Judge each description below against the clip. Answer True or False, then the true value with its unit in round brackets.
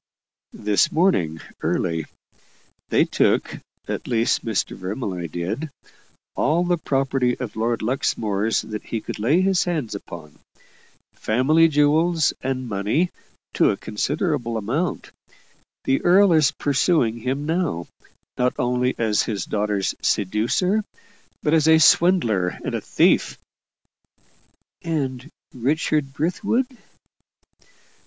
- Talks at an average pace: False (115 wpm)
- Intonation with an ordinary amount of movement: False (6.8 semitones)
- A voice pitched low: True (130 Hz)